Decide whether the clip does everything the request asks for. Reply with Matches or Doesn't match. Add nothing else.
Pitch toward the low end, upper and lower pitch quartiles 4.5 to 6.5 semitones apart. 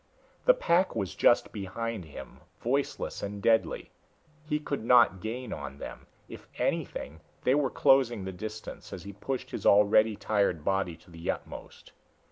Matches